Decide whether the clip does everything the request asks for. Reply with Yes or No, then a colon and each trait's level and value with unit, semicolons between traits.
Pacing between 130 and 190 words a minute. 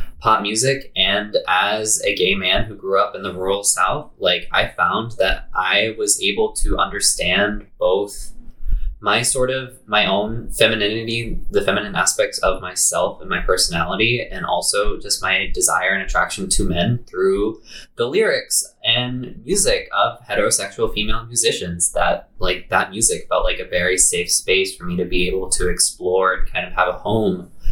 Yes: average, 170 wpm